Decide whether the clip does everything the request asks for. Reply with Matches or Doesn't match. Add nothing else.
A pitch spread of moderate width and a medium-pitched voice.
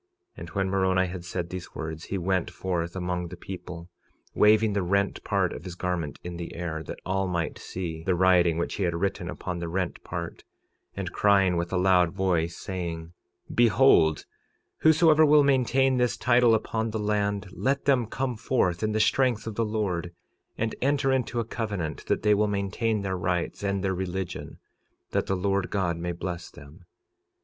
Doesn't match